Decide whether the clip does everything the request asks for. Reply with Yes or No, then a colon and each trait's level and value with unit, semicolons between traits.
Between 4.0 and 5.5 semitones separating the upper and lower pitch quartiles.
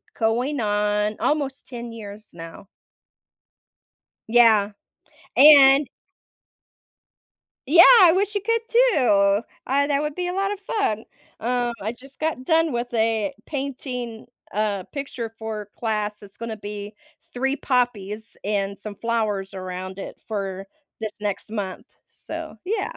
Yes: average, 5.1 semitones